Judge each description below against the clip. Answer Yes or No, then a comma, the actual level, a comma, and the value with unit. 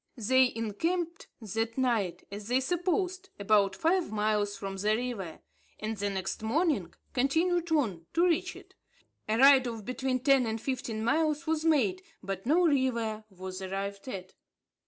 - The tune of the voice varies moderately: No, wide, 7.0 semitones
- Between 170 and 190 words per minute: No, average, 155 wpm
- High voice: Yes, high, 235 Hz